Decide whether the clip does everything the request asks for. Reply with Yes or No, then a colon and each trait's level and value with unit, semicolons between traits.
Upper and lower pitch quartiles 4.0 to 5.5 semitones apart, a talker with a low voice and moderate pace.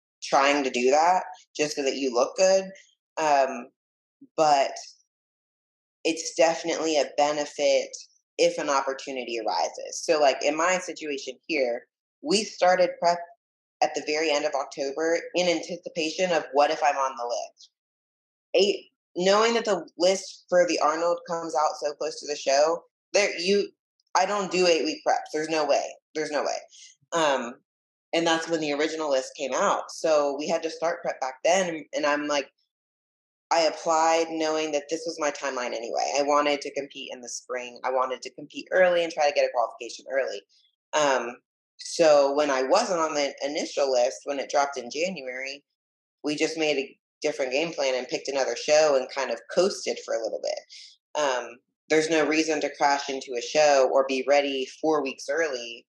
No: average, 4.3 semitones; medium, 155 Hz; average, 185 wpm